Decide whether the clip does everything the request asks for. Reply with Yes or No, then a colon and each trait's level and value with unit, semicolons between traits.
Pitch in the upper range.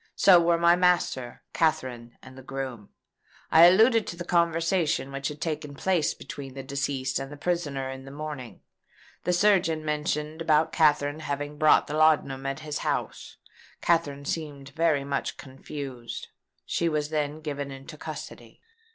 No: medium, 150 Hz